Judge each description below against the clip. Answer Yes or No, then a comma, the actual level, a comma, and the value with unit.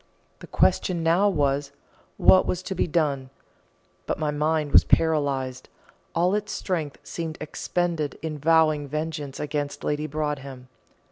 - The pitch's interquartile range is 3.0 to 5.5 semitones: No, narrow, 2.4 semitones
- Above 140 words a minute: No, slow, 135 wpm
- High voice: No, medium, 155 Hz